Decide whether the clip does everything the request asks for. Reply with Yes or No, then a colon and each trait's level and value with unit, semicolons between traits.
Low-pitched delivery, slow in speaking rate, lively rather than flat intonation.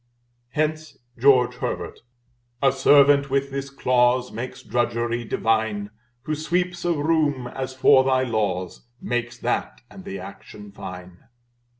No: low, 130 Hz; slow, 125 wpm; average, 3.7 semitones